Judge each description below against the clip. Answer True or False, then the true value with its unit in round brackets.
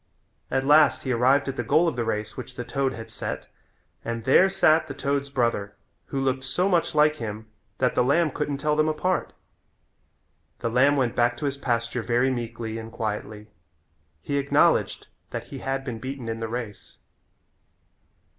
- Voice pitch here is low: True (130 Hz)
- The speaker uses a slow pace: False (180 wpm)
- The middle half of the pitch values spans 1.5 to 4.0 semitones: True (3.5 semitones)